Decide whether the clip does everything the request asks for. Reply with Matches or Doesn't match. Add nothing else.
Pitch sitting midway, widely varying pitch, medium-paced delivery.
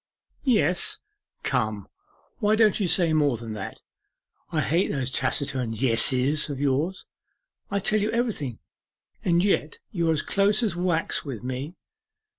Matches